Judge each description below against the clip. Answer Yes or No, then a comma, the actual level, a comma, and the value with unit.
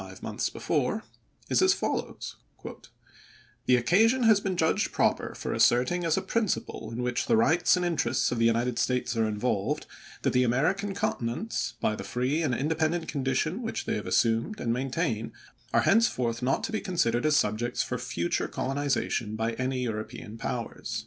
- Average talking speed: Yes, average, 175 wpm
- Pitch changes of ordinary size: No, wide, 7.1 semitones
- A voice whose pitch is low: Yes, low, 125 Hz